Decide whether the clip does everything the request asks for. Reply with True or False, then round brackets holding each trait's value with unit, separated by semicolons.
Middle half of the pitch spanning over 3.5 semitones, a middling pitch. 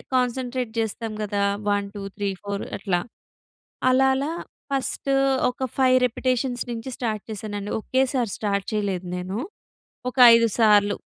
False (3.9 semitones; 225 Hz)